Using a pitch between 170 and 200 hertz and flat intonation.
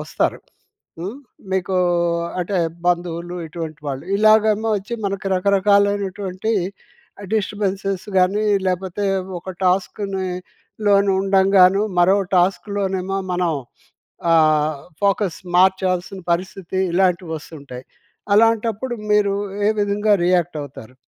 Yes: high, 190 Hz; narrow, 2.2 semitones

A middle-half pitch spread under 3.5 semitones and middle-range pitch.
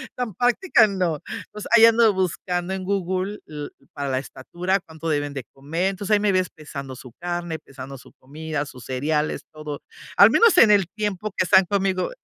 No: average, 5.2 semitones; medium, 175 Hz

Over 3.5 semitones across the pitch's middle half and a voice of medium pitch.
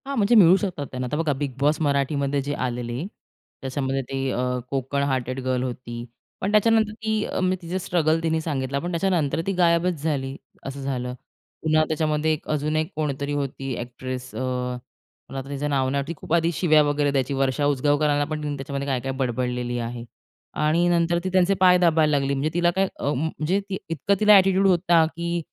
Yes: average, 4.2 semitones; medium, 145 Hz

